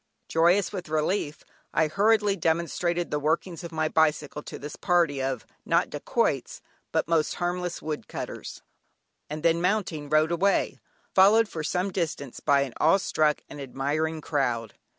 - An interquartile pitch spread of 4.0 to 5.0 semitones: No, average, 3.1 semitones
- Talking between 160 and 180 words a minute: No, average, 150 wpm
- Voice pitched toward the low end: No, medium, 160 Hz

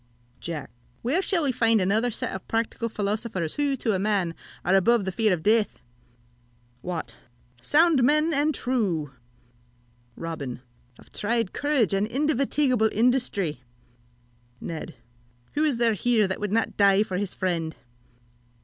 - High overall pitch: Yes, high, 220 Hz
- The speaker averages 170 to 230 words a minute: No, average, 145 wpm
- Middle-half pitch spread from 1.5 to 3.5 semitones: No, average, 5.0 semitones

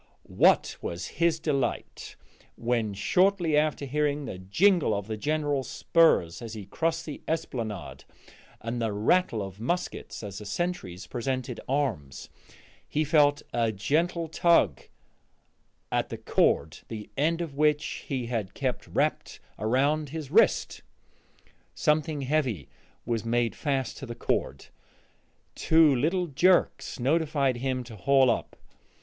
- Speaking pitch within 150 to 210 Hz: No, low, 135 Hz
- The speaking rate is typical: No, slow, 130 wpm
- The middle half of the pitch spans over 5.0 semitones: Yes, wide, 5.5 semitones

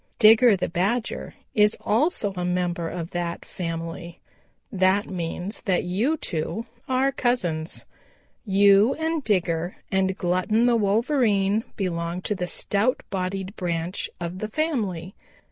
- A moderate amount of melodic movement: Yes, average, 4.1 semitones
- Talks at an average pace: No, slow, 130 wpm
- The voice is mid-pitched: No, high, 195 Hz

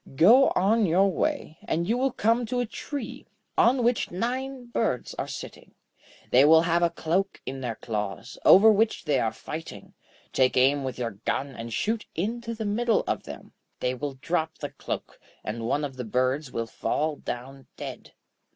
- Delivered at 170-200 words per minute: Yes, average, 180 wpm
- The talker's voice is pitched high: No, medium, 160 Hz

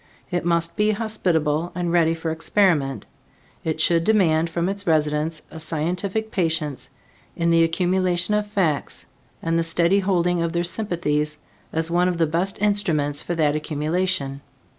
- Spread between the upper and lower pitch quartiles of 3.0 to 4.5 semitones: No, narrow, 2.5 semitones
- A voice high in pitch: No, medium, 170 Hz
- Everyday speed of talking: Yes, average, 155 wpm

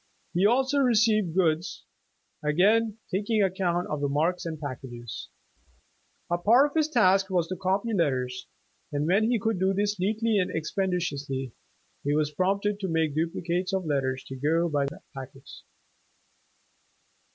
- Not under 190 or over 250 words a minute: No, average, 155 wpm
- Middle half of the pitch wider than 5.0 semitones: Yes, wide, 5.5 semitones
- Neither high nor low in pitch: Yes, medium, 180 Hz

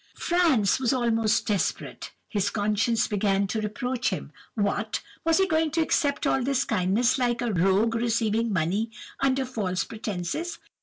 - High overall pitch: Yes, high, 225 Hz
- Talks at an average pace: Yes, average, 150 wpm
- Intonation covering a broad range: No, average, 4.1 semitones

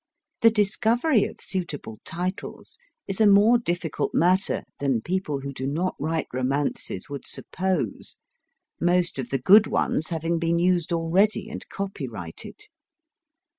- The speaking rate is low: Yes, slow, 130 wpm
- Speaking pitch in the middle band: Yes, medium, 170 Hz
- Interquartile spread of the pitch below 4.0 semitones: No, wide, 5.6 semitones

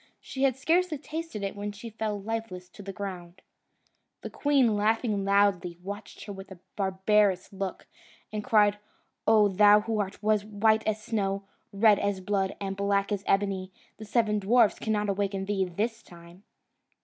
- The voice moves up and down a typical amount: No, narrow, 1.9 semitones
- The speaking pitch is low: No, high, 205 Hz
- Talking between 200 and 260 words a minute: No, average, 160 wpm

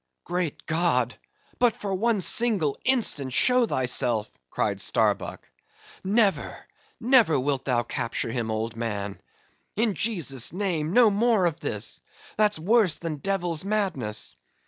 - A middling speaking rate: No, slow, 125 wpm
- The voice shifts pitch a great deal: Yes, wide, 8.5 semitones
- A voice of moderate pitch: Yes, medium, 170 Hz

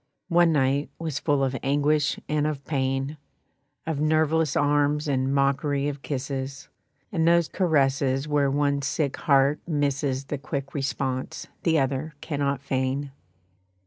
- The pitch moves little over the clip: Yes, narrow, 1.9 semitones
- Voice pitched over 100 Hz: Yes, medium, 140 Hz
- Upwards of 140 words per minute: No, slow, 135 wpm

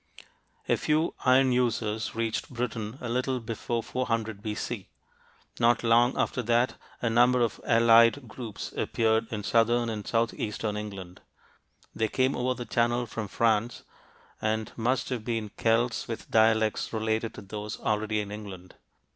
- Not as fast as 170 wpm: Yes, average, 145 wpm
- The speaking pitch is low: Yes, low, 115 Hz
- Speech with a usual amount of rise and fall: No, narrow, 1.9 semitones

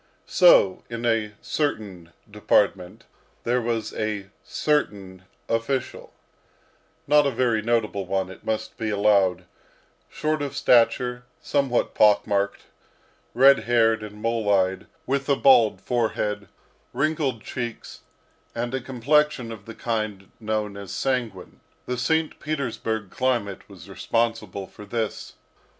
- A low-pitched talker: Yes, low, 115 Hz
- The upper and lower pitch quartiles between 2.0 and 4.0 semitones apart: Yes, average, 3.7 semitones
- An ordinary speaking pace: No, slow, 125 wpm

